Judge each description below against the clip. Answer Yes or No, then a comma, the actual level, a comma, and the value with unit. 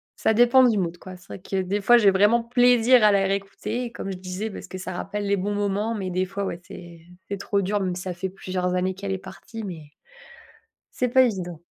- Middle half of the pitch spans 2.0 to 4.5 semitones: Yes, average, 2.8 semitones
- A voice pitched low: No, high, 195 Hz